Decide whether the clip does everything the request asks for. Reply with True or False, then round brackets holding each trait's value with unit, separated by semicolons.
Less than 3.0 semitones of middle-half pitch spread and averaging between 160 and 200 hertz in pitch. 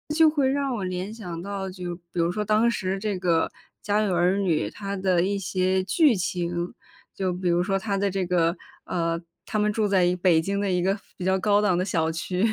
True (2.4 semitones; 190 Hz)